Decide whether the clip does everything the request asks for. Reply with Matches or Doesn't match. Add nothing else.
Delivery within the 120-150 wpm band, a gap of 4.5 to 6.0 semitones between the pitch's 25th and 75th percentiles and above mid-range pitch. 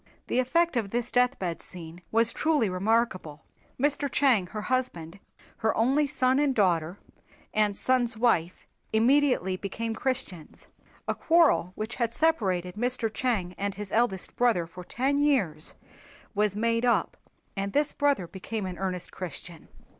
Matches